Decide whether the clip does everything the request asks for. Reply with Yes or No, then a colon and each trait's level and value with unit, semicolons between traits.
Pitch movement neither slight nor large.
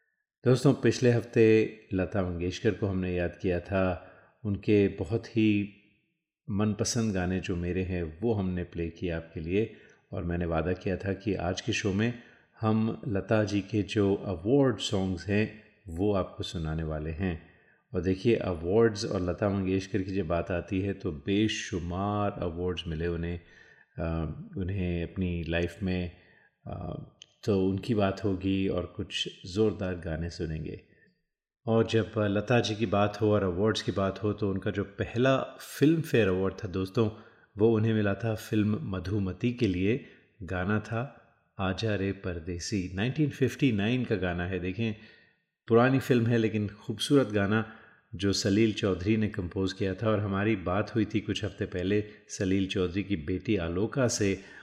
Yes: average, 3.2 semitones